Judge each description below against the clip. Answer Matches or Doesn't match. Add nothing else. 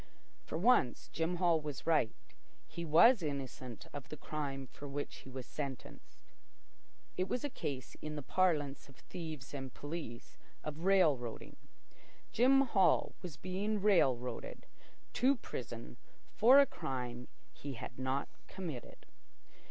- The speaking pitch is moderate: Matches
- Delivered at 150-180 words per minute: Doesn't match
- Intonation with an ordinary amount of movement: Doesn't match